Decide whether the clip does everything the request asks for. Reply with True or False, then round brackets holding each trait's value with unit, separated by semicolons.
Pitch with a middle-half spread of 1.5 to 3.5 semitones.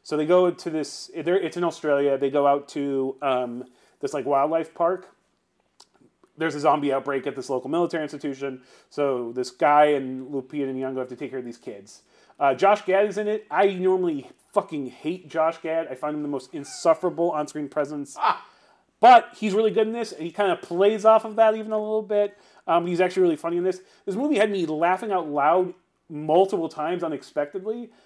False (5.2 semitones)